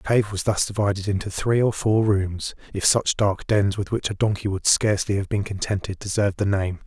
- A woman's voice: No, male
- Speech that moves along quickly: Yes, fast, 225 wpm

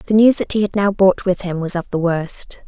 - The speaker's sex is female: Yes, female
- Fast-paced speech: Yes, fast, 290 wpm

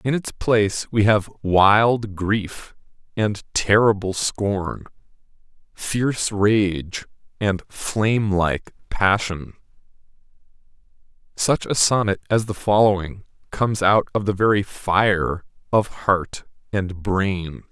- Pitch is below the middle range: Yes, low, 100 Hz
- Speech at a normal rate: No, slow, 110 wpm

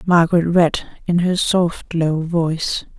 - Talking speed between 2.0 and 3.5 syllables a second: No, 3.8 syllables/s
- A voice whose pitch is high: No, medium, 170 Hz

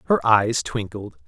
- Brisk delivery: No, average, 140 wpm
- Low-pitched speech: Yes, low, 105 Hz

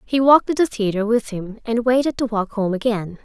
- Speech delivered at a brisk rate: Yes, fast, 240 wpm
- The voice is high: Yes, high, 225 Hz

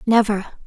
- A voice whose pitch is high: Yes, high, 210 Hz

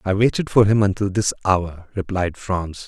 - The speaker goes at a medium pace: Yes, average, 190 wpm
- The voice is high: No, very low, 95 Hz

